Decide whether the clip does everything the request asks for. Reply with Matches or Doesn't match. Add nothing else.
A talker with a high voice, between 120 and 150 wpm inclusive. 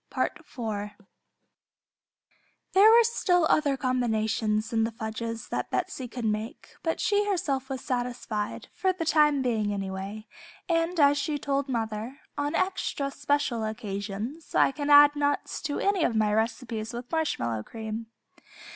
Matches